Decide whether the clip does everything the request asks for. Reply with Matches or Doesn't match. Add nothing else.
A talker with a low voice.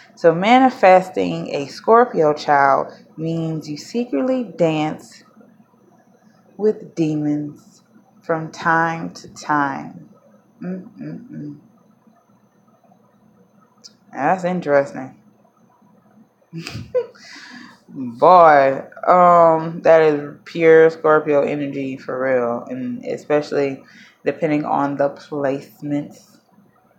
Doesn't match